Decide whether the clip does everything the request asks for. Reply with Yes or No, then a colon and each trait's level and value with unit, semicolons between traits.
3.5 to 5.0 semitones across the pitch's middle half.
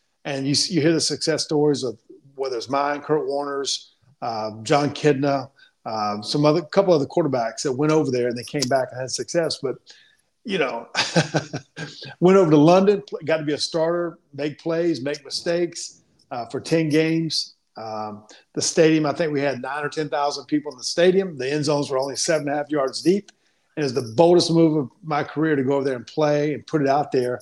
No: average, 2.9 semitones